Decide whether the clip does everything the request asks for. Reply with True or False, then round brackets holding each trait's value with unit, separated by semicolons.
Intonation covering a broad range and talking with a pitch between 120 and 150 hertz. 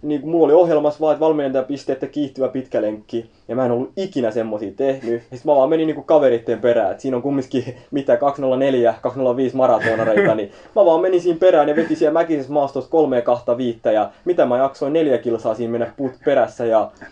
False (3.6 semitones; 135 Hz)